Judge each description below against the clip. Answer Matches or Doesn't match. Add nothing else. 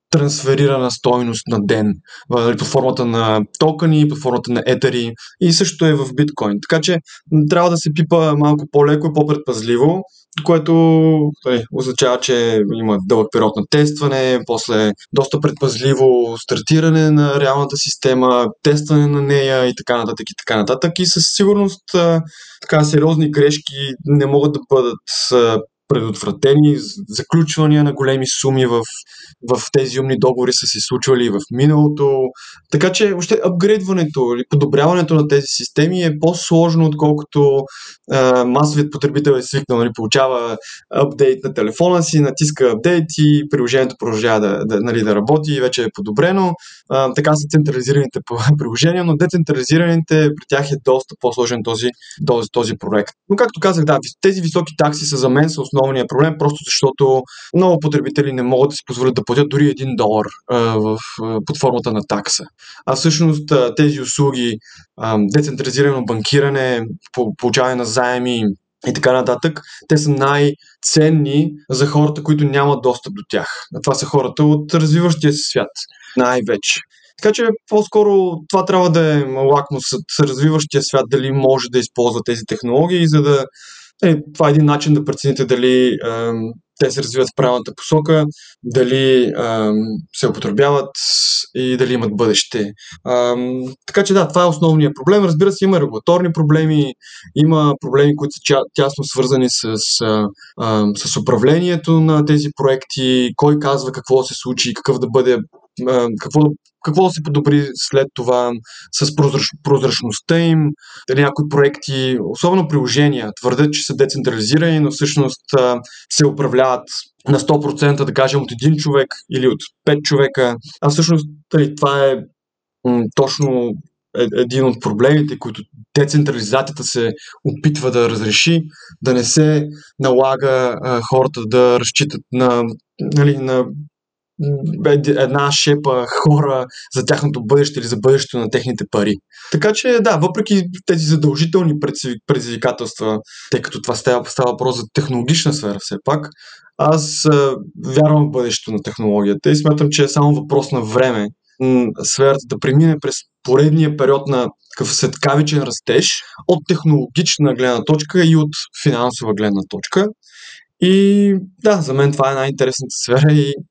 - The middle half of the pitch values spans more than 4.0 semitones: Doesn't match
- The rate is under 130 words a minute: Doesn't match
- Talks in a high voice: Doesn't match